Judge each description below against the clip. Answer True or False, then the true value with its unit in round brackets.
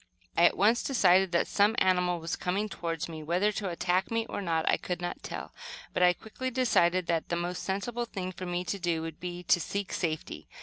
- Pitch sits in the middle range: True (180 Hz)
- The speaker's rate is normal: False (220 wpm)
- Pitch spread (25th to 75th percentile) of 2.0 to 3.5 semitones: True (2.7 semitones)